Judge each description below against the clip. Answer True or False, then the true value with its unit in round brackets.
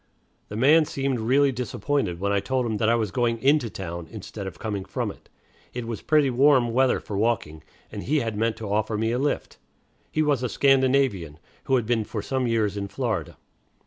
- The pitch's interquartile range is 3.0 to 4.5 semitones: True (4.1 semitones)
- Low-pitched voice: True (115 Hz)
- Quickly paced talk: True (210 wpm)